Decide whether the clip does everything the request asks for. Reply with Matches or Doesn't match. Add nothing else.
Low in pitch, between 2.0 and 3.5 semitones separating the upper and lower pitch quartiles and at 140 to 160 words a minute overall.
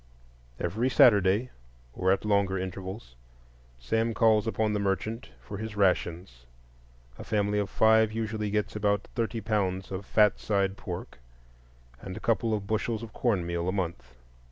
Matches